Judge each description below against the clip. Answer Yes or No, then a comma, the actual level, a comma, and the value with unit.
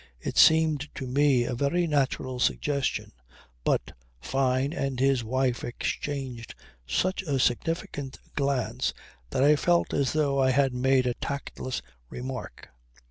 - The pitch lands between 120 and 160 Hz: Yes, low, 135 Hz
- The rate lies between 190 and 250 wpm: No, slow, 135 wpm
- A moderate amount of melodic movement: No, narrow, 2.2 semitones